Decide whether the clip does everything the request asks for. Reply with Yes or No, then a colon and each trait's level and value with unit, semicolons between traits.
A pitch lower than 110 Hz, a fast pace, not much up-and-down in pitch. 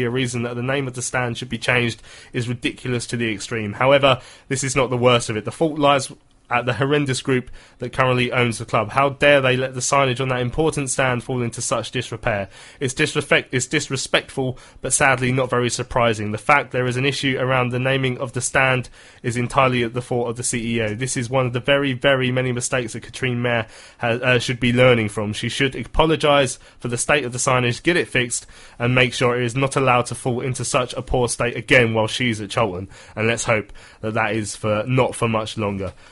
No: low, 125 Hz; fast, 230 wpm; narrow, 2.0 semitones